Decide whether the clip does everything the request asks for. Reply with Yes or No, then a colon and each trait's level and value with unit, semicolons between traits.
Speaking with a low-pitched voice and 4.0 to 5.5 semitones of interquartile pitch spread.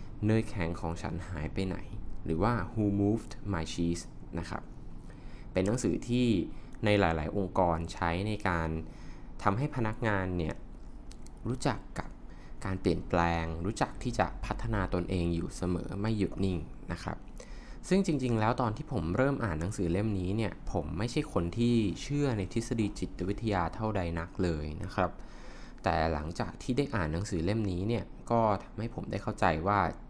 Yes: low, 100 Hz; average, 4.5 semitones